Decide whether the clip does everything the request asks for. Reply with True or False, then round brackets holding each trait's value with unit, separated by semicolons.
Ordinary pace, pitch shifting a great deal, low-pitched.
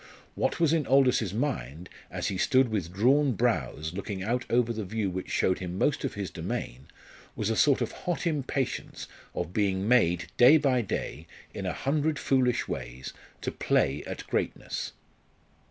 True (170 wpm; 6.5 semitones; 110 Hz)